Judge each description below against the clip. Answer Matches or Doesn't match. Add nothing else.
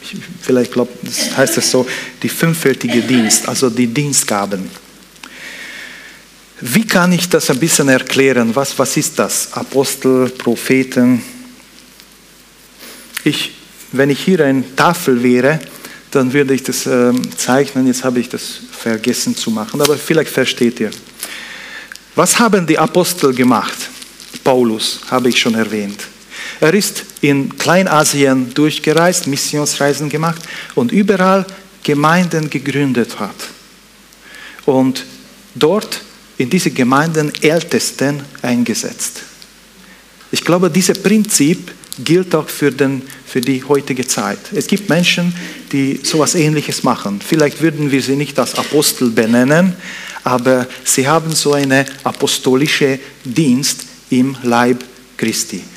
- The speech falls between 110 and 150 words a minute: Matches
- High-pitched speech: Doesn't match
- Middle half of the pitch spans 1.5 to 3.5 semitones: Doesn't match